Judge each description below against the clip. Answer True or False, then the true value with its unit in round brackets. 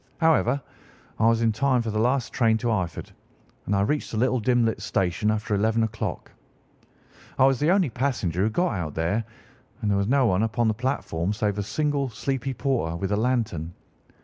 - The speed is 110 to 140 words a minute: False (200 wpm)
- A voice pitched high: False (115 Hz)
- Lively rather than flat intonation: False (4.0 semitones)